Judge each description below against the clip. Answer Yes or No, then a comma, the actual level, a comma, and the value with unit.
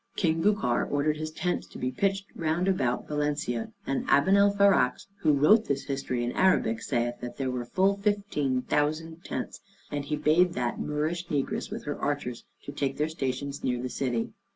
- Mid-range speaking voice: Yes, medium, 150 Hz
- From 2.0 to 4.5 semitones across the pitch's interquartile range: No, average, 5.2 semitones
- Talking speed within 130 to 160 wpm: No, average, 175 wpm